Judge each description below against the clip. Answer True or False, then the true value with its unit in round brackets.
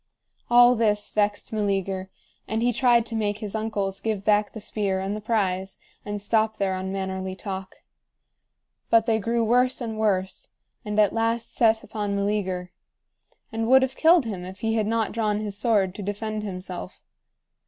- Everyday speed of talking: True (170 wpm)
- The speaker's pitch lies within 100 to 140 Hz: False (210 Hz)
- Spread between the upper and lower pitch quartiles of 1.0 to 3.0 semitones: True (2.6 semitones)